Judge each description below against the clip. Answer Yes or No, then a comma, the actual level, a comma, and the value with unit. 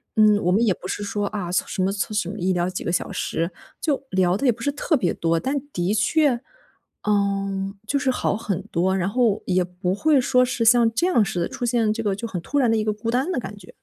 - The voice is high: Yes, high, 210 Hz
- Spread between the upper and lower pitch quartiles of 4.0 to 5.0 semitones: Yes, average, 4.4 semitones